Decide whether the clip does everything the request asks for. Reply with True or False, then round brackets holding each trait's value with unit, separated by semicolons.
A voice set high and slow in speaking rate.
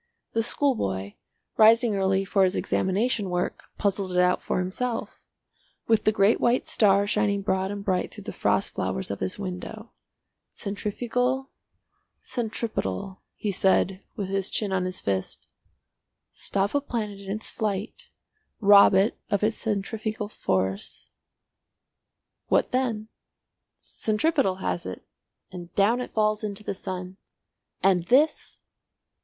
True (200 Hz; 130 wpm)